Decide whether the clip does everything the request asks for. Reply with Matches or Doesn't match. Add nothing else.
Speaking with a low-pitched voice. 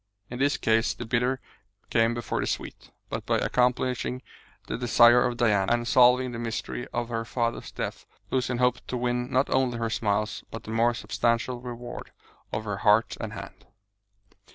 Matches